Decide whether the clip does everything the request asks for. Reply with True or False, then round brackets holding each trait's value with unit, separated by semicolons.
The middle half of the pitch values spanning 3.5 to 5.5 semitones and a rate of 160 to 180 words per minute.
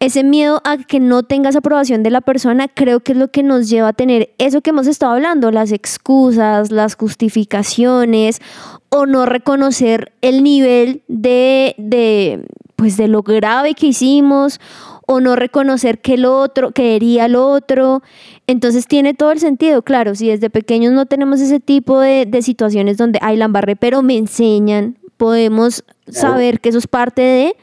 False (3.1 semitones; 170 wpm)